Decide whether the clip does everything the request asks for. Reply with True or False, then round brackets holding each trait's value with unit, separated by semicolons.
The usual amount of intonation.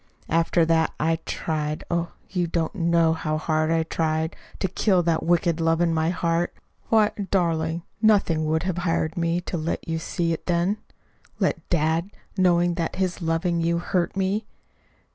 False (1.4 semitones)